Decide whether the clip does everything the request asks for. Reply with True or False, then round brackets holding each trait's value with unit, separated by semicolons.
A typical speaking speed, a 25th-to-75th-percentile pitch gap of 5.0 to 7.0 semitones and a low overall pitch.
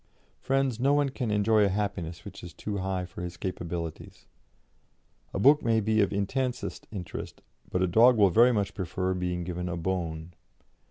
False (175 wpm; 4.2 semitones; 95 Hz)